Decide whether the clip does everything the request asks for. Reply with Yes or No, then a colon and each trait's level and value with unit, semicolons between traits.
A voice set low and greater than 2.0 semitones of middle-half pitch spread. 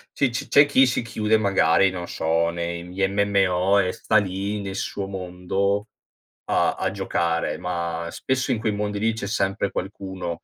Yes: very low, 95 Hz; narrow, 2.6 semitones